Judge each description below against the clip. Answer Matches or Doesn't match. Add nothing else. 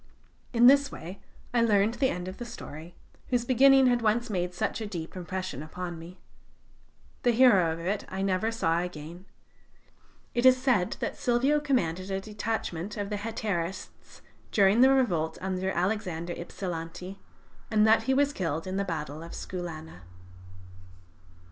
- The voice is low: Doesn't match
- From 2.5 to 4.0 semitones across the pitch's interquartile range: Doesn't match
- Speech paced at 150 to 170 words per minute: Matches